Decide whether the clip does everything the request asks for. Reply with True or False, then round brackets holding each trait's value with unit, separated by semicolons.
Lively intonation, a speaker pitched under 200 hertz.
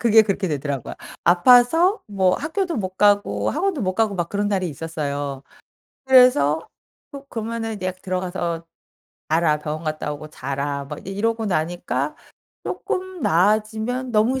True (6.6 semitones; 190 Hz)